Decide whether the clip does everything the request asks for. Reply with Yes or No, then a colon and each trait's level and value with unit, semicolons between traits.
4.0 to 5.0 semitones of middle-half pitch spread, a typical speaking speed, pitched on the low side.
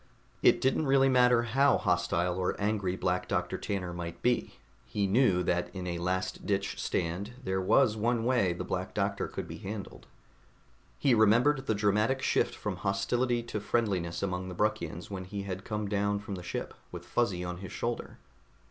Yes: average, 4.5 semitones; average, 180 wpm; low, 100 Hz